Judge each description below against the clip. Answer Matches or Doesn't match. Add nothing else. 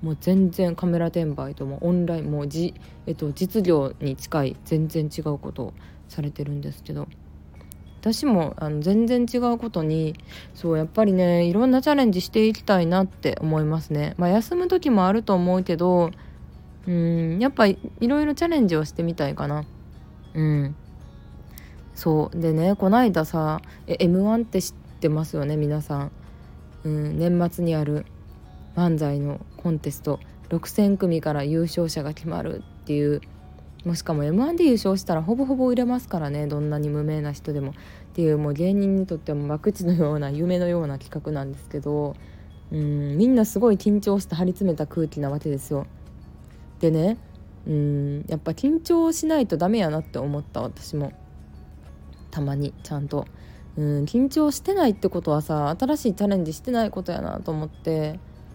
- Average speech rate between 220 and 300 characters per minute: Doesn't match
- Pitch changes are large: Doesn't match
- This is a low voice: Doesn't match